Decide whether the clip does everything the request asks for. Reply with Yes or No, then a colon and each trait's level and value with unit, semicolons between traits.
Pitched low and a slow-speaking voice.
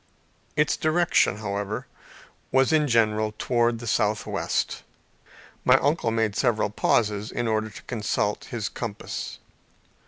Yes: low, 115 Hz; slow, 120 wpm